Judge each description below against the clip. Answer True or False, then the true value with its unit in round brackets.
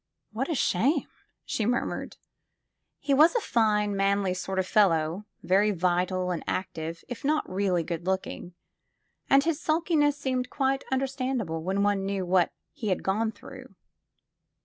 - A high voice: True (205 Hz)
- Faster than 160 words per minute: False (150 wpm)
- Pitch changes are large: True (6.4 semitones)